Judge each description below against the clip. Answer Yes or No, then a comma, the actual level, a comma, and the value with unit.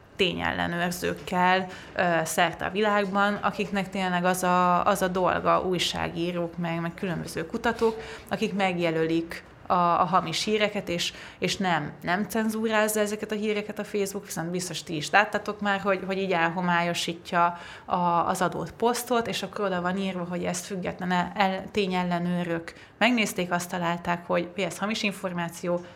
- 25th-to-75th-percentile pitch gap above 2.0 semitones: Yes, average, 2.8 semitones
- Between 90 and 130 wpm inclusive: No, average, 145 wpm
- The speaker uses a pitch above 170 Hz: Yes, medium, 185 Hz